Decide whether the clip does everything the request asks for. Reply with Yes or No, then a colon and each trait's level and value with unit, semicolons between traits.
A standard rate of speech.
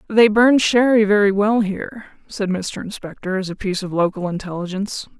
Yes: average, 175 wpm